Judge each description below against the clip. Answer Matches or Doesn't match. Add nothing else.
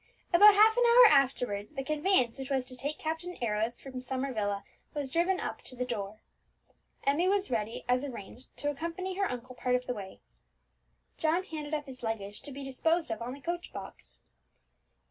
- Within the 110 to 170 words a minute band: Doesn't match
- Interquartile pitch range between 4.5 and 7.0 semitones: Matches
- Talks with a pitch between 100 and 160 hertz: Doesn't match